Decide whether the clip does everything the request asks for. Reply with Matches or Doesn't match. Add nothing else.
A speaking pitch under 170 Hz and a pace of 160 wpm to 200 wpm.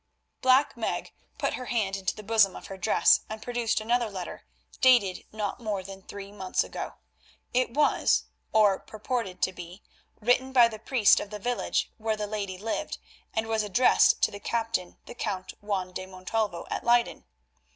Doesn't match